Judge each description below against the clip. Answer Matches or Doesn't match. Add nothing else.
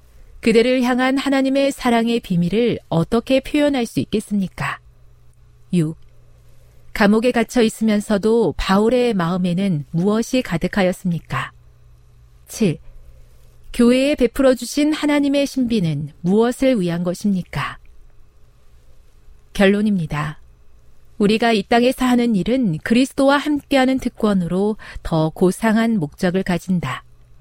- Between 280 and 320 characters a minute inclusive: Doesn't match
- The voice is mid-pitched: Doesn't match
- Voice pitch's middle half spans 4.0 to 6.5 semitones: Doesn't match